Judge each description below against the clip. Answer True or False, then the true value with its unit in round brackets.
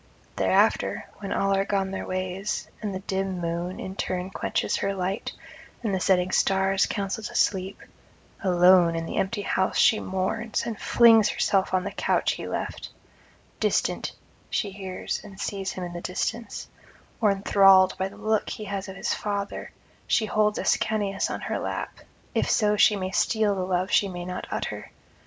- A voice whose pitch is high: True (195 Hz)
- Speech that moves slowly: False (175 wpm)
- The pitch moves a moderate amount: False (1.7 semitones)